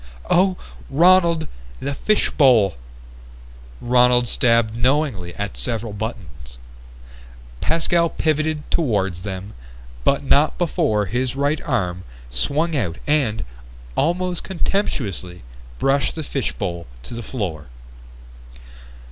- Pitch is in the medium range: No, low, 125 Hz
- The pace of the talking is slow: Yes, slow, 95 wpm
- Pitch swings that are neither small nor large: No, wide, 7.6 semitones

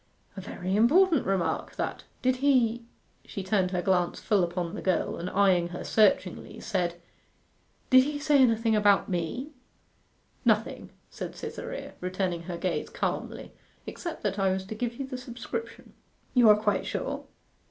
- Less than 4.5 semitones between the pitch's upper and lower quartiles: No, average, 5.0 semitones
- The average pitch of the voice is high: Yes, high, 205 Hz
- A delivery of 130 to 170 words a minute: Yes, average, 160 wpm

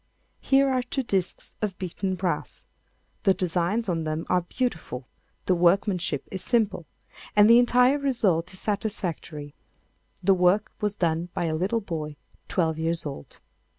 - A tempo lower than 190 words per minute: Yes, average, 150 wpm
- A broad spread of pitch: No, average, 4.3 semitones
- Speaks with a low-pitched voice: No, medium, 185 Hz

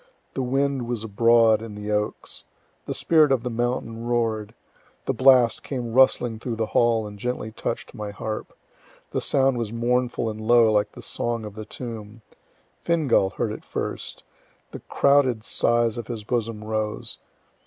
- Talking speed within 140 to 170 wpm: Yes, average, 165 wpm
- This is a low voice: Yes, low, 115 Hz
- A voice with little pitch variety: Yes, narrow, 2.3 semitones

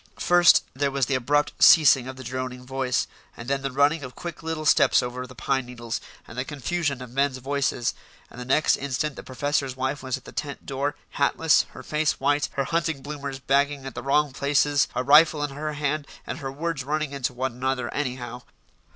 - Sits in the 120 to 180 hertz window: Yes, medium, 140 Hz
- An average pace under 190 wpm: No, fast, 205 wpm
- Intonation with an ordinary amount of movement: No, narrow, 2.3 semitones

